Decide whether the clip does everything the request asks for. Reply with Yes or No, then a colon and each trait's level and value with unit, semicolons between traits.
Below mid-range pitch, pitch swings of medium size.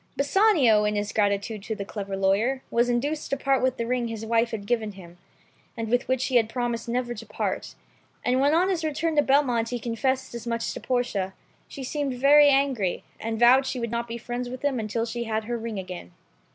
No: high, 240 Hz; average, 3.1 semitones